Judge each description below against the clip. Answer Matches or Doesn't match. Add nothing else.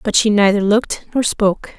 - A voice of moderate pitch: Doesn't match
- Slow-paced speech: Doesn't match